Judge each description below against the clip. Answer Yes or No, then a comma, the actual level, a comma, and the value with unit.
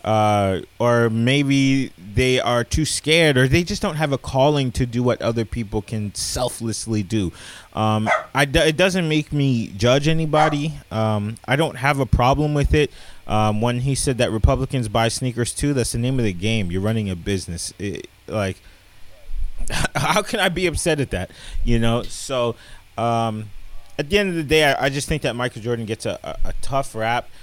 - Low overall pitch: Yes, low, 120 Hz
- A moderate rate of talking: Yes, average, 195 wpm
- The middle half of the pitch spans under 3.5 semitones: No, average, 4.6 semitones